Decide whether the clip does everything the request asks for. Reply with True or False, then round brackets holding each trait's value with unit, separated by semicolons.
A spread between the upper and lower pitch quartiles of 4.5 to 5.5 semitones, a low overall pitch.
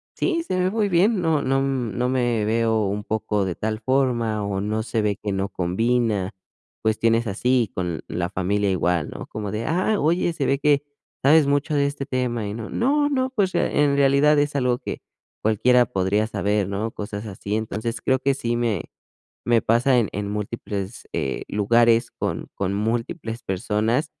True (5.0 semitones; 115 Hz)